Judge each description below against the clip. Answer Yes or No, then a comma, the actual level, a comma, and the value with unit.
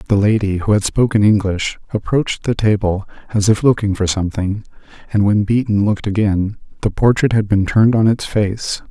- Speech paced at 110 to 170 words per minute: No, average, 180 wpm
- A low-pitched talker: Yes, low, 105 Hz